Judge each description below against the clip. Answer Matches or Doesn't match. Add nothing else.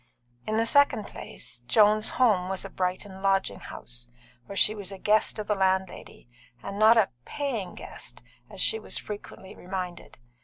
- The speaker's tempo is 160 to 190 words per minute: Matches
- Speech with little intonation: Matches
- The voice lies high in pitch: Matches